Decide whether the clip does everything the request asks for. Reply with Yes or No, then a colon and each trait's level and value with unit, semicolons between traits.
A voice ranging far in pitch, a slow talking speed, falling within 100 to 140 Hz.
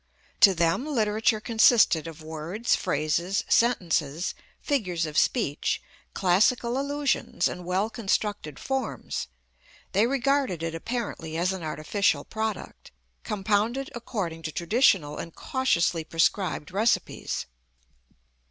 No: wide, 6.2 semitones; slow, 105 wpm; high, 195 Hz